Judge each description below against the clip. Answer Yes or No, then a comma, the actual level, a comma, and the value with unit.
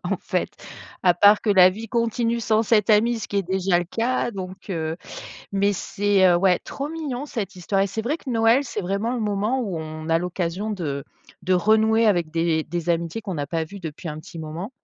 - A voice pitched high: Yes, high, 195 Hz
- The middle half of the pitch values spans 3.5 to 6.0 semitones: Yes, average, 4.5 semitones